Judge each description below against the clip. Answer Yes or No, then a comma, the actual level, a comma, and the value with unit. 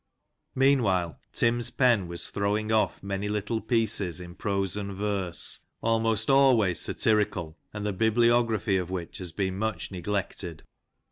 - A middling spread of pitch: Yes, average, 3.2 semitones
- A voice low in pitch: Yes, low, 105 Hz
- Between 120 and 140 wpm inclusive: Yes, slow, 135 wpm